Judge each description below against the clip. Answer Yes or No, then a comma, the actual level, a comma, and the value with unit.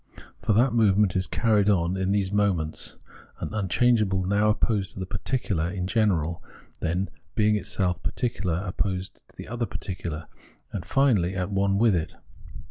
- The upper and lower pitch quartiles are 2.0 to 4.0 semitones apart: Yes, average, 2.8 semitones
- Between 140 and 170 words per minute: Yes, average, 155 wpm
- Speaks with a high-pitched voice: No, low, 100 Hz